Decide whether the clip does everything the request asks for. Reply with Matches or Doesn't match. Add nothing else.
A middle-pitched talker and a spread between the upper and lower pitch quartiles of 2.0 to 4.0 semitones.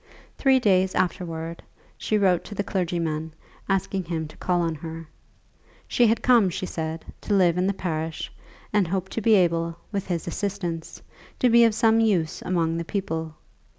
Matches